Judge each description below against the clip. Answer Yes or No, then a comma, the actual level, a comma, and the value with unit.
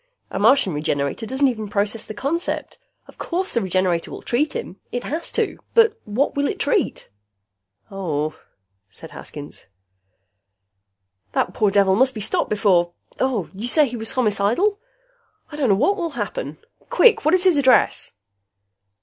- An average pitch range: No, wide, 7.2 semitones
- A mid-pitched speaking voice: No, high, 235 Hz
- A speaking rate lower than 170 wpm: Yes, average, 155 wpm